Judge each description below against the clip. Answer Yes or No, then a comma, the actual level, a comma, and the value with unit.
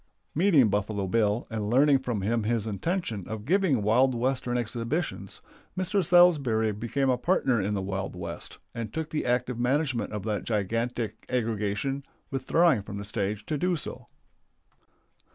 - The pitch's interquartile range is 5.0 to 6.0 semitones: No, average, 4.6 semitones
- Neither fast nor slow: Yes, average, 150 wpm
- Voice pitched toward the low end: Yes, low, 120 Hz